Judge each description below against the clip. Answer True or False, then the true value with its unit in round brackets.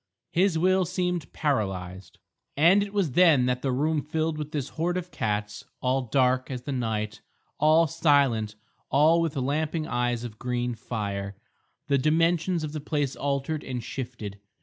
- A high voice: False (140 Hz)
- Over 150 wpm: True (160 wpm)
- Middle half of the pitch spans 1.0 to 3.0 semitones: False (4.8 semitones)